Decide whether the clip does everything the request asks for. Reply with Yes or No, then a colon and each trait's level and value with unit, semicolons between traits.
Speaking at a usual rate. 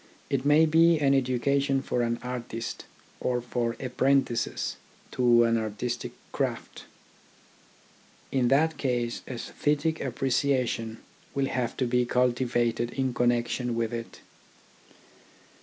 No: slow, 115 wpm